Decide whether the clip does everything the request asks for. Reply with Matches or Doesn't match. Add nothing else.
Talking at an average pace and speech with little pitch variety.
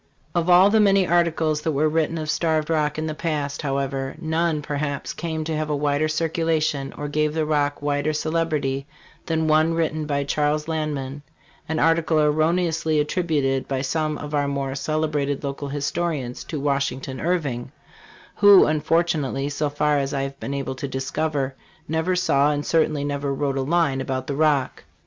Matches